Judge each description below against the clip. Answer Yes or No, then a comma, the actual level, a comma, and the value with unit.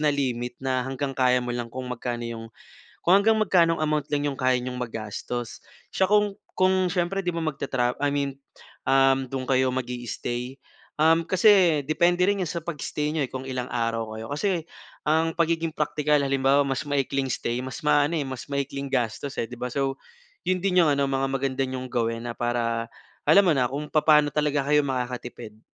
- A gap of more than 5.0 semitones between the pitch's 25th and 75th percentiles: No, average, 3.8 semitones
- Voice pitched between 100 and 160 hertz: Yes, low, 135 Hz